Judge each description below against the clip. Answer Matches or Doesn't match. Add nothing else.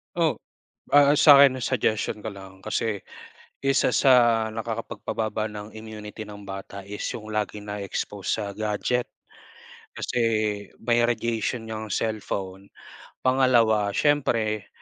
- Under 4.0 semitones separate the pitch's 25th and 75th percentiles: Matches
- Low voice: Matches